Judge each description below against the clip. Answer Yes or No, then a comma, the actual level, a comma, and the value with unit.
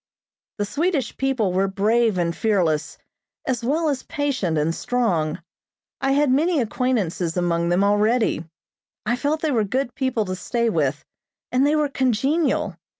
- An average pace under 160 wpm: Yes, average, 150 wpm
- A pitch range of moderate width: No, wide, 6.6 semitones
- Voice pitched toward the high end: Yes, high, 230 Hz